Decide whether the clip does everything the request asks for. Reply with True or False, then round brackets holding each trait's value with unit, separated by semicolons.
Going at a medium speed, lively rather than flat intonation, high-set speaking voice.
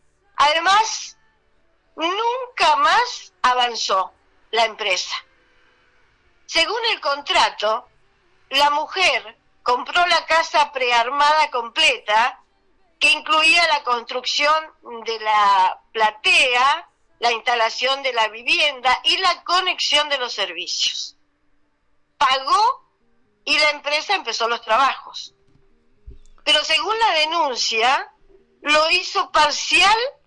False (95 wpm; 6.5 semitones; 300 Hz)